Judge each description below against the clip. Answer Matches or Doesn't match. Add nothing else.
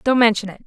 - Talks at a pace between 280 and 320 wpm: Doesn't match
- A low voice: Doesn't match